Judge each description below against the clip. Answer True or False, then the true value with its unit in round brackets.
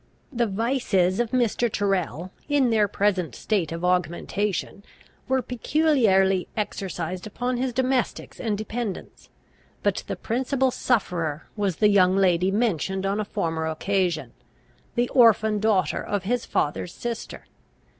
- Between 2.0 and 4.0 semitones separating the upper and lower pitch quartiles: False (4.6 semitones)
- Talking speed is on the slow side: True (130 wpm)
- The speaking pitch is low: False (205 Hz)